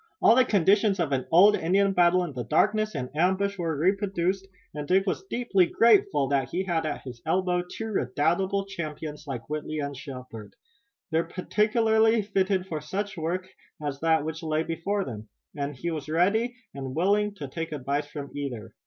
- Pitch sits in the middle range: Yes, medium, 170 Hz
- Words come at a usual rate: Yes, average, 180 wpm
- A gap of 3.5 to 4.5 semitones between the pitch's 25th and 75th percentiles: No, average, 5.1 semitones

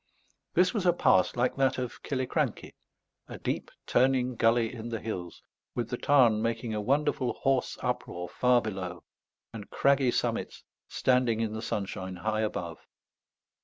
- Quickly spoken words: No, average, 150 wpm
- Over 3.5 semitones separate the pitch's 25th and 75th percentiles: No, average, 3.1 semitones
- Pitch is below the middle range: Yes, low, 120 Hz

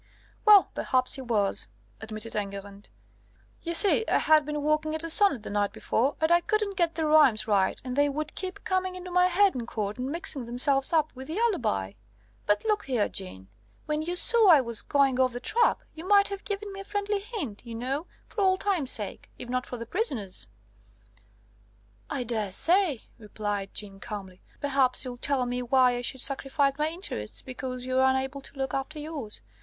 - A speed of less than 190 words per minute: No, average, 195 wpm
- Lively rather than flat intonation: Yes, wide, 6.6 semitones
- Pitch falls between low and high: No, very high, 270 Hz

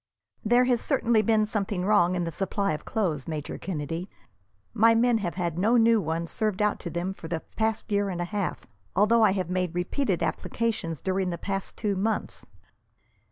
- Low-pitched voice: No, high, 195 Hz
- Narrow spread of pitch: No, average, 4.0 semitones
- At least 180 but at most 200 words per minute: Yes, average, 190 wpm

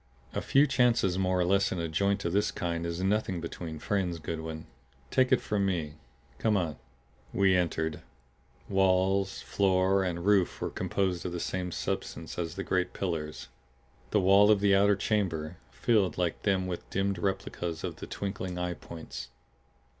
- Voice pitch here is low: Yes, very low, 95 Hz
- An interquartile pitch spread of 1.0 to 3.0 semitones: Yes, narrow, 2.4 semitones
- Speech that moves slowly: No, average, 170 wpm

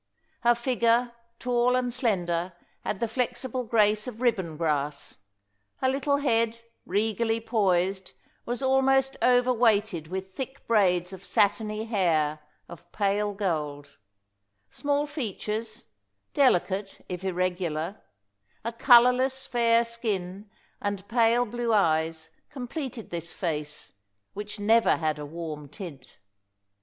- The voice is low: No, high, 215 Hz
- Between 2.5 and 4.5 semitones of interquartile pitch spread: No, average, 5.3 semitones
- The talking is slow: Yes, slow, 115 wpm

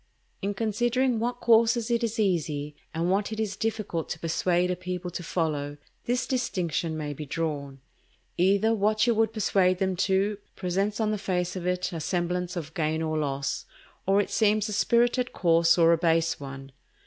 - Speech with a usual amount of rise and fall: Yes, average, 4.7 semitones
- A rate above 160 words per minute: Yes, average, 185 wpm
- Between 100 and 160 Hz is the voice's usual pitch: No, medium, 185 Hz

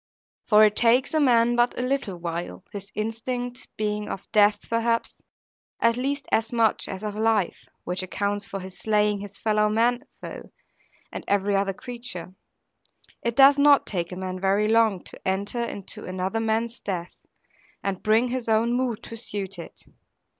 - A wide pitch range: No, average, 3.2 semitones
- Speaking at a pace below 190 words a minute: Yes, average, 170 wpm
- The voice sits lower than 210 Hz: No, high, 215 Hz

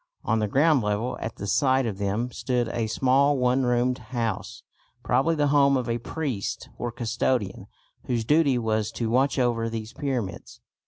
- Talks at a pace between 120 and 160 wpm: No, average, 170 wpm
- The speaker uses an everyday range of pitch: Yes, average, 3.1 semitones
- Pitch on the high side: No, low, 120 Hz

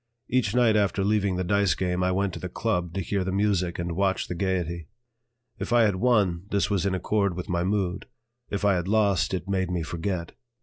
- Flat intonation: Yes, narrow, 2.3 semitones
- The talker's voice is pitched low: Yes, very low, 95 Hz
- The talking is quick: Yes, fast, 220 wpm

